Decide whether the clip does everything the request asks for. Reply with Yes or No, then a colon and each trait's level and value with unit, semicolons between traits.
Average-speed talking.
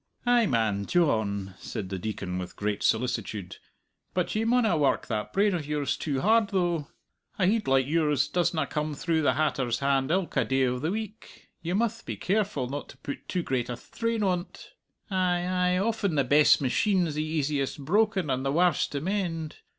Yes: average, 185 wpm